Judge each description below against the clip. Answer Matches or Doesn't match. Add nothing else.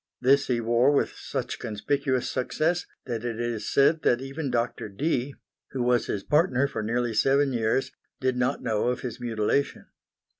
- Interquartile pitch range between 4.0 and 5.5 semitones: Doesn't match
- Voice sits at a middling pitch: Doesn't match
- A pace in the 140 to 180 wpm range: Matches